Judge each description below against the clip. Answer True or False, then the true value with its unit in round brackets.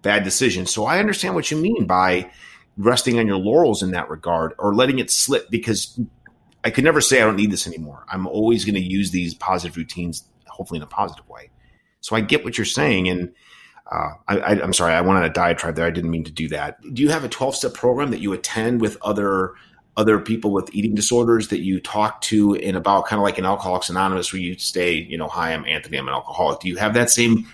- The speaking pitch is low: True (100 Hz)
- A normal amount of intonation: True (3.9 semitones)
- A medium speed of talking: False (245 wpm)